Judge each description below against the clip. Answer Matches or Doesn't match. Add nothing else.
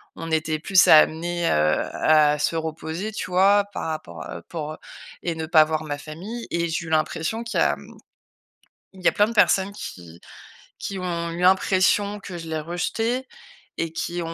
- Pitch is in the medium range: Matches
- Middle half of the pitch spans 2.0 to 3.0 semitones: Doesn't match